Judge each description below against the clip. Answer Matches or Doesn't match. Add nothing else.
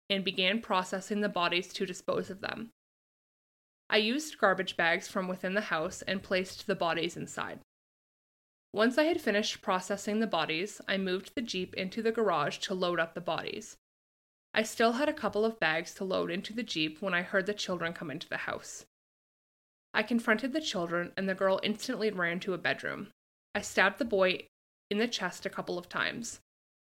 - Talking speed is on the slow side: Doesn't match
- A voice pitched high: Matches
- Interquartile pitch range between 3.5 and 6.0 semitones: Doesn't match